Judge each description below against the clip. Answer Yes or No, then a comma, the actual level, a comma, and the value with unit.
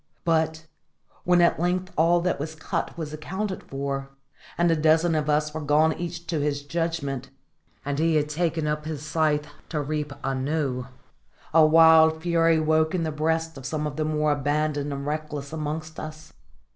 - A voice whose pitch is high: No, medium, 155 Hz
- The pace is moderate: Yes, average, 175 wpm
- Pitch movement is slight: Yes, narrow, 1.7 semitones